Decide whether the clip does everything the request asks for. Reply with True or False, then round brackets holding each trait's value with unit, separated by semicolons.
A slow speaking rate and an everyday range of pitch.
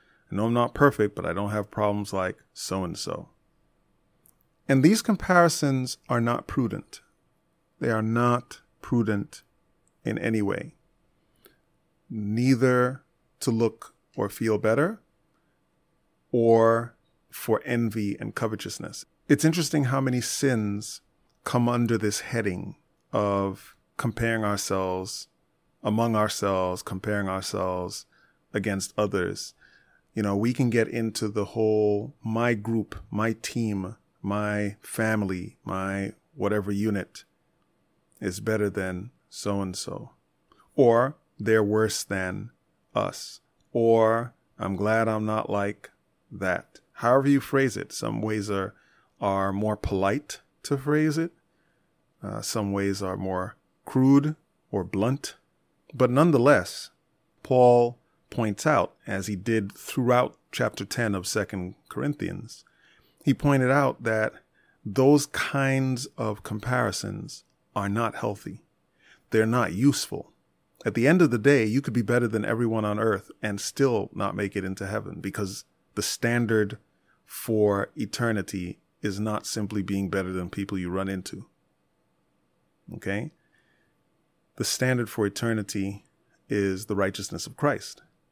True (125 wpm; 3.3 semitones)